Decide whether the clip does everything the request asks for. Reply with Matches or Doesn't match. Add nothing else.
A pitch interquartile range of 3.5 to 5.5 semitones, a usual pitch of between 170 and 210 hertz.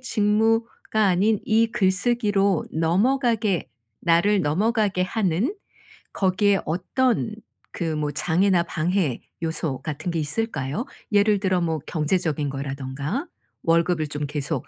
Matches